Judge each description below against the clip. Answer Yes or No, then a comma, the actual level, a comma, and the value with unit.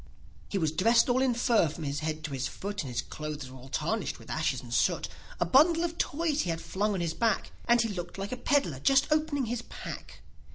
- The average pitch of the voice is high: Yes, high, 205 Hz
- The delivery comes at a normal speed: No, fast, 240 wpm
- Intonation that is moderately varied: No, wide, 8.7 semitones